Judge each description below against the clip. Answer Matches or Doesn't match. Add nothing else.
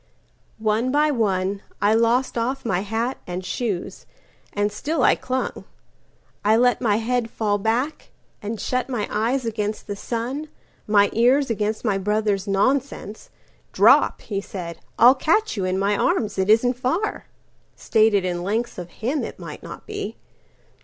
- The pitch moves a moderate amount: Matches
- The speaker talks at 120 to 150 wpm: Matches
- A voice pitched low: Doesn't match